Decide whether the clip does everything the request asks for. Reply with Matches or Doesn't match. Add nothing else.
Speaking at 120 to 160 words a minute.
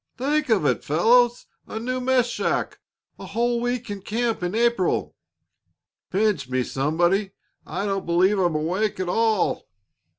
Matches